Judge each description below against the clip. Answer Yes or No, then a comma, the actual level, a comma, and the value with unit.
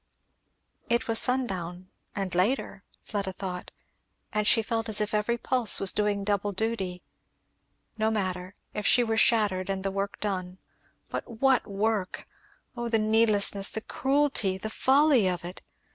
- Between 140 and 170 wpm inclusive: Yes, average, 150 wpm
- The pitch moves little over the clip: No, average, 3.0 semitones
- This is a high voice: Yes, high, 210 Hz